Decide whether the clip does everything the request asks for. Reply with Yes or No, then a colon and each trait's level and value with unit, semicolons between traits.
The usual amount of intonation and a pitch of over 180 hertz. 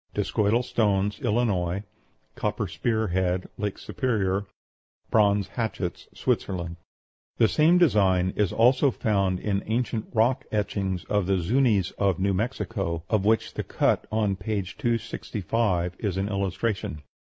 No: average, 3.1 semitones; low, 100 Hz